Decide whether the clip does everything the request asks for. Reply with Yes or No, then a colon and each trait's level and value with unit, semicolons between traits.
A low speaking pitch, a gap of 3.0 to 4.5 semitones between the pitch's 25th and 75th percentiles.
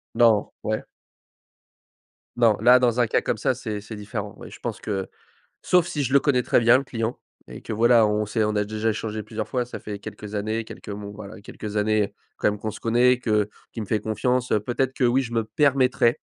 No: low, 110 Hz; narrow, 2.6 semitones